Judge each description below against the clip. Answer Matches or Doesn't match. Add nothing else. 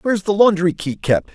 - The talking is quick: Matches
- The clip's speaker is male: Matches